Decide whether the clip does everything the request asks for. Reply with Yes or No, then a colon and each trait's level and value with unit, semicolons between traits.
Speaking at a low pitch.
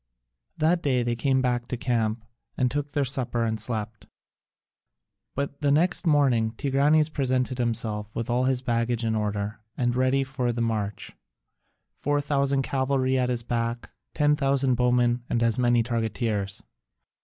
Yes: low, 125 Hz